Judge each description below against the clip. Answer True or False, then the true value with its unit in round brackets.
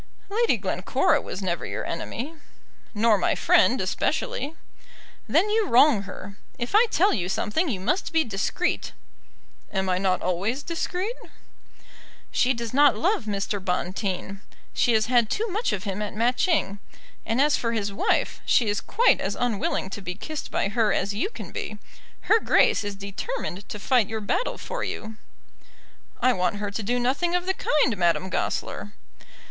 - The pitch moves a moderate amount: False (7.6 semitones)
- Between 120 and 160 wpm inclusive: False (170 wpm)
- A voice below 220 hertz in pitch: False (225 Hz)